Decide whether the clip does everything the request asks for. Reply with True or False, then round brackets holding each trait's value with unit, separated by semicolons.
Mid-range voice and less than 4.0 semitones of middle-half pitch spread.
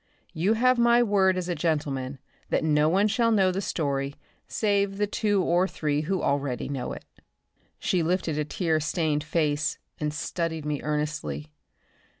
False (160 Hz; 4.7 semitones)